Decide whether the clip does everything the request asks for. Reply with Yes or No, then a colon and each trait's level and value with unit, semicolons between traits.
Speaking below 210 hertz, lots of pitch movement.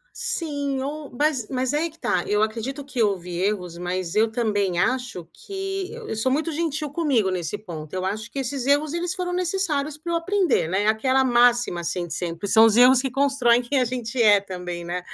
No: high, 245 Hz; wide, 6.8 semitones